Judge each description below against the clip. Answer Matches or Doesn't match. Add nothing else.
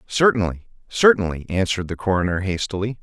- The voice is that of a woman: Doesn't match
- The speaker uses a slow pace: Matches